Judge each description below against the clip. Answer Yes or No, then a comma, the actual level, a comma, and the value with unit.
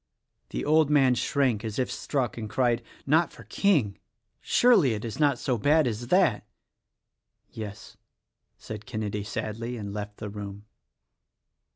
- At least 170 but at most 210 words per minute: No, average, 145 wpm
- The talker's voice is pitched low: Yes, low, 120 Hz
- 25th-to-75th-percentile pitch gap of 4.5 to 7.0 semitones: Yes, average, 5.0 semitones